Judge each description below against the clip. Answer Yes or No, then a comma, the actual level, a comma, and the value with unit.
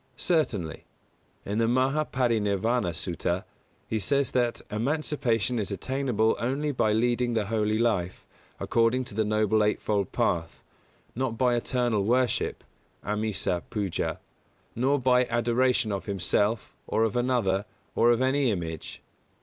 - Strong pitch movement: No, average, 3.4 semitones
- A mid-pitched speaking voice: No, low, 115 Hz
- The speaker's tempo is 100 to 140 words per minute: Yes, slow, 135 wpm